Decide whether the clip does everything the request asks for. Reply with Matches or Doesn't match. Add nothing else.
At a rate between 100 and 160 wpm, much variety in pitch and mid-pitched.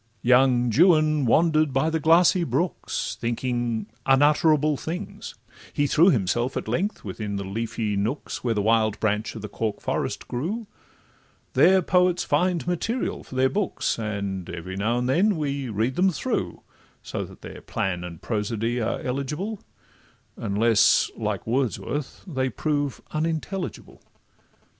Doesn't match